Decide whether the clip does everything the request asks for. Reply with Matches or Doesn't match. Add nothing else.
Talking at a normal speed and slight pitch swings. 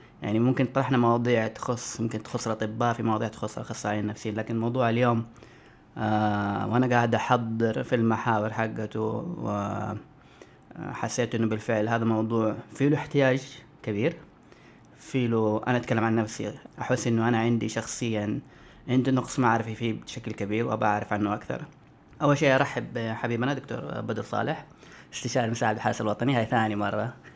Doesn't match